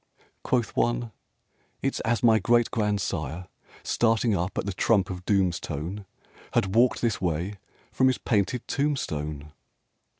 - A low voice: Yes, low, 105 Hz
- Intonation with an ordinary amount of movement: Yes, average, 4.7 semitones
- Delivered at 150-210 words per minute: No, slow, 135 wpm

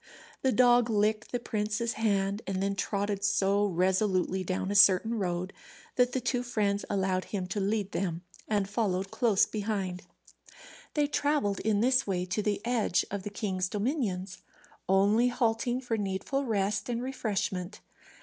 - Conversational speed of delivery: Yes, average, 155 wpm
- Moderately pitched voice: No, high, 205 Hz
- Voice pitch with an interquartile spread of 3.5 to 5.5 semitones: No, average, 3.1 semitones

